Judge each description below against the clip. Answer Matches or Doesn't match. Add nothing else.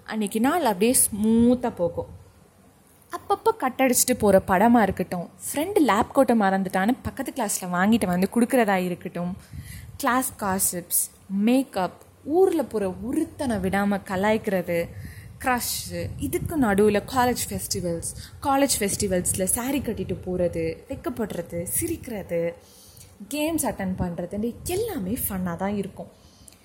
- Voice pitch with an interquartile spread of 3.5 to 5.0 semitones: Doesn't match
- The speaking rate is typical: Matches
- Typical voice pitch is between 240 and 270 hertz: Doesn't match